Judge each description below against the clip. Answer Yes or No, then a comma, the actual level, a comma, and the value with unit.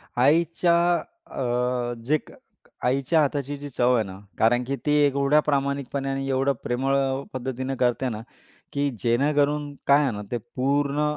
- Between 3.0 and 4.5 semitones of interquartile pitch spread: No, narrow, 2.6 semitones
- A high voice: No, low, 135 Hz